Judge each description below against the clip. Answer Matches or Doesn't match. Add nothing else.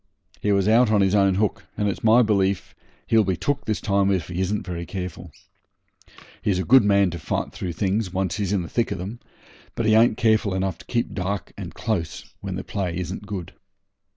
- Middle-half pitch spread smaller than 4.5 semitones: Matches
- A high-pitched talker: Doesn't match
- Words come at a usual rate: Doesn't match